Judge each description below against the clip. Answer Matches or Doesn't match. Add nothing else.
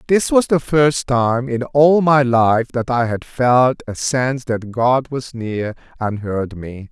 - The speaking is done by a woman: Doesn't match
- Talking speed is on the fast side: Doesn't match